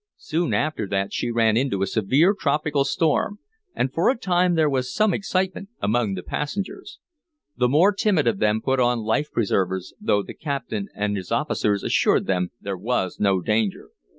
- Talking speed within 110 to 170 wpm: No, average, 180 wpm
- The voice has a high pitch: No, low, 125 Hz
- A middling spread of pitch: No, wide, 8.0 semitones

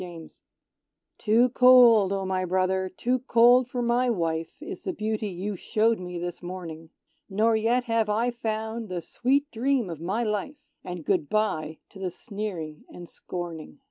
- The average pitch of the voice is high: Yes, high, 210 Hz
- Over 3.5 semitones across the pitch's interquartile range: Yes, average, 4.9 semitones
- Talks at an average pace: Yes, average, 165 wpm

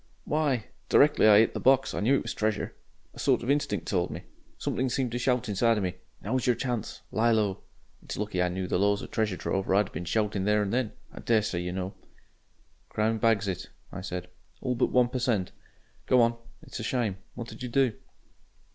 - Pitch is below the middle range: Yes, low, 110 Hz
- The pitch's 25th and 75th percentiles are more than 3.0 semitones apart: Yes, average, 3.8 semitones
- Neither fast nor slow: No, fast, 225 wpm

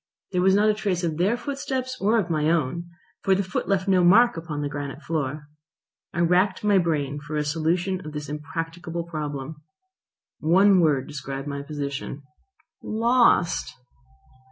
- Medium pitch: Yes, medium, 165 Hz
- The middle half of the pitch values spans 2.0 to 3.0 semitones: No, average, 4.4 semitones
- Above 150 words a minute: Yes, average, 160 wpm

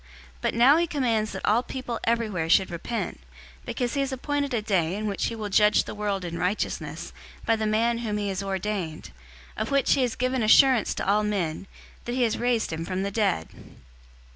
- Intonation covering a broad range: No, average, 3.7 semitones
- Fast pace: Yes, fast, 215 wpm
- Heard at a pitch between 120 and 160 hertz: No, high, 215 Hz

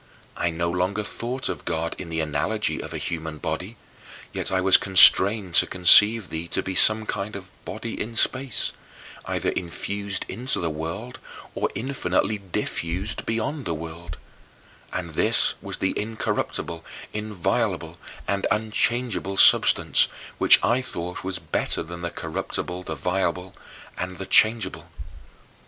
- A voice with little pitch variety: No, average, 4.2 semitones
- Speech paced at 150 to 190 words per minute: No, average, 140 wpm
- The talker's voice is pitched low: Yes, very low, 95 Hz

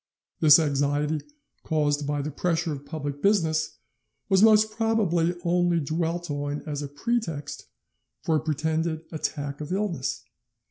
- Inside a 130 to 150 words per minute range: Yes, slow, 135 wpm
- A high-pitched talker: No, medium, 160 Hz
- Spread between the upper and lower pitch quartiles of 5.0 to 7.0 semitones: No, average, 3.2 semitones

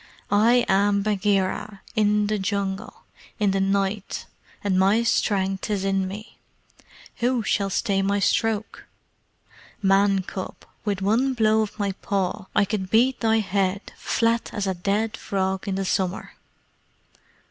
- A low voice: No, high, 200 Hz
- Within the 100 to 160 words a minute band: Yes, average, 140 wpm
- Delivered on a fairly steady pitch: Yes, narrow, 1.9 semitones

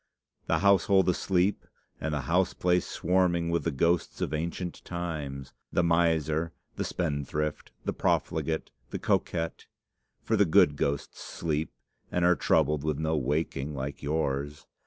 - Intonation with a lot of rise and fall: No, average, 3.0 semitones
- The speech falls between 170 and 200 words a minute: No, average, 140 wpm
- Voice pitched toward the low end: Yes, very low, 80 Hz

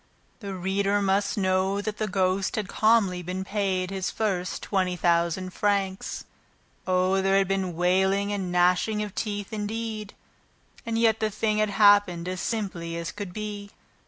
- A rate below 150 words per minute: No, average, 160 wpm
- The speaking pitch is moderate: No, high, 195 Hz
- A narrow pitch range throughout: Yes, narrow, 2.1 semitones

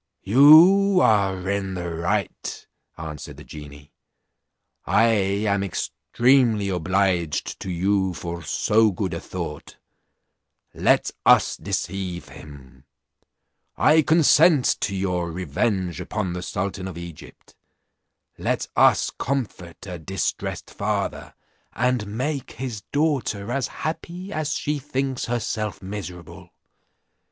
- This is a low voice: Yes, low, 100 Hz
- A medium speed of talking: No, slow, 110 wpm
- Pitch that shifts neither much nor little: No, wide, 6.3 semitones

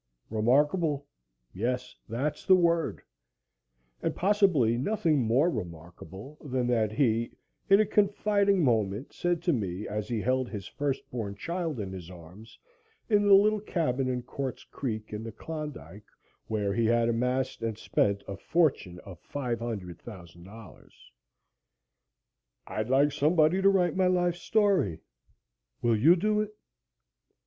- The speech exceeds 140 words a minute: No, slow, 135 wpm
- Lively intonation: Yes, wide, 8.0 semitones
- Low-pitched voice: Yes, low, 125 Hz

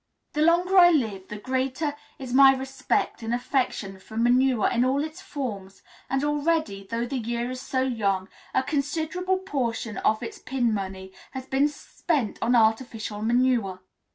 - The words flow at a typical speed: Yes, average, 160 wpm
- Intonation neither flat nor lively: Yes, average, 4.5 semitones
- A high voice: Yes, very high, 255 Hz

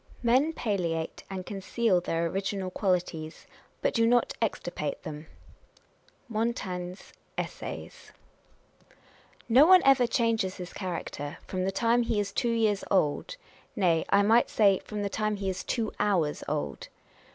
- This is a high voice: Yes, high, 200 Hz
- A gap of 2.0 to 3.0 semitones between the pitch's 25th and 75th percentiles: No, average, 4.2 semitones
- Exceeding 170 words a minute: No, average, 140 wpm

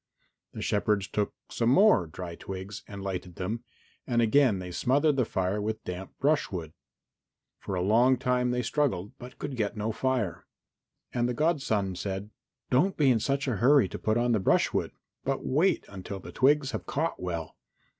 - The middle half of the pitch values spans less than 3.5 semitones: No, wide, 5.4 semitones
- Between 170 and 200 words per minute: Yes, average, 175 wpm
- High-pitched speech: No, low, 110 Hz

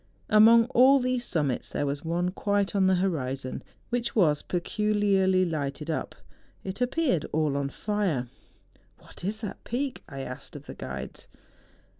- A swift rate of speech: No, average, 160 wpm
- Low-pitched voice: No, medium, 185 Hz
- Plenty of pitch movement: Yes, wide, 6.4 semitones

